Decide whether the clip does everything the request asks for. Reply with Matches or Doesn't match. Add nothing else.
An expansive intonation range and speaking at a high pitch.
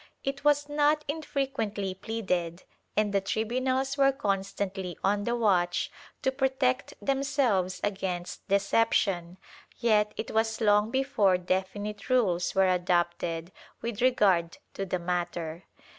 Matches